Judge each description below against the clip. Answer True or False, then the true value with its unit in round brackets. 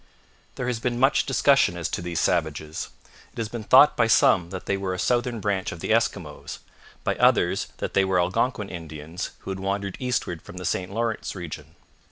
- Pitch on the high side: False (95 Hz)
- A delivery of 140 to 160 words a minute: False (200 wpm)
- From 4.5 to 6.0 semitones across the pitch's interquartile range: True (5.0 semitones)